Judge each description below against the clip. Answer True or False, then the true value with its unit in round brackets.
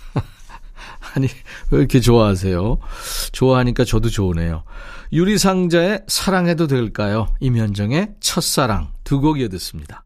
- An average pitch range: False (8.4 semitones)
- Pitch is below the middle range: True (130 Hz)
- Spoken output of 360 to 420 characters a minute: False (285 characters per minute)